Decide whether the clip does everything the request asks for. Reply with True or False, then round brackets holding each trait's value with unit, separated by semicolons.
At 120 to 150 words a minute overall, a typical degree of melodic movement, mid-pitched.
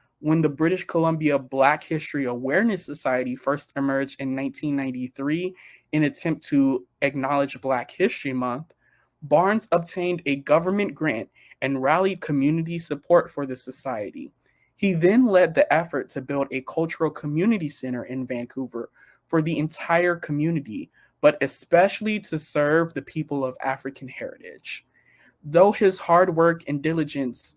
True (140 wpm; 3.9 semitones; 145 Hz)